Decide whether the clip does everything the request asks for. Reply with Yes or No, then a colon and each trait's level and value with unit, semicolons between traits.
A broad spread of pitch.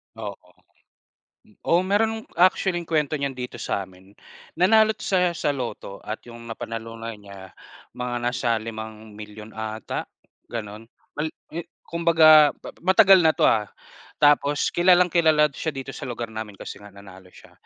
Yes: wide, 7.5 semitones